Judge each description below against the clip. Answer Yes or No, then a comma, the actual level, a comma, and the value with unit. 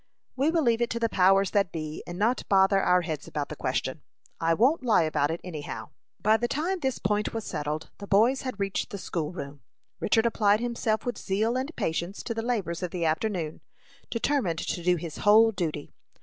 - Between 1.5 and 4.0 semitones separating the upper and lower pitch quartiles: No, wide, 5.4 semitones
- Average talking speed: No, fast, 210 wpm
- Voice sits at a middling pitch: No, high, 200 Hz